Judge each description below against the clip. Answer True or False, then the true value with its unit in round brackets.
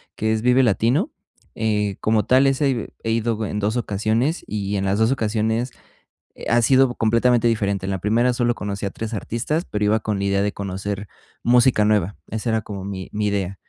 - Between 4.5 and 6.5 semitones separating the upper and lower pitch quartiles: False (2.9 semitones)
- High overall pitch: False (110 Hz)